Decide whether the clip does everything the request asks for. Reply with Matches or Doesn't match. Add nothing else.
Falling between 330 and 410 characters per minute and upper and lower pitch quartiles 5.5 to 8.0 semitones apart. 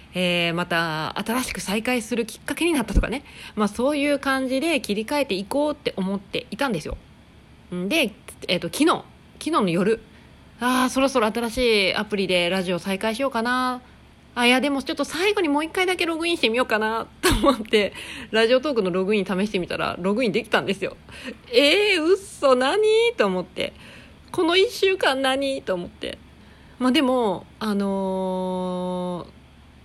Matches